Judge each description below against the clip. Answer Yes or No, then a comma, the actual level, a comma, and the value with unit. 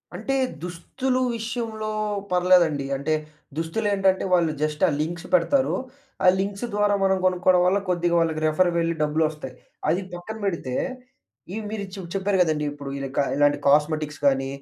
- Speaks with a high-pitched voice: No, medium, 175 Hz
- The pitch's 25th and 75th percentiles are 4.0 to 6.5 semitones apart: Yes, average, 4.4 semitones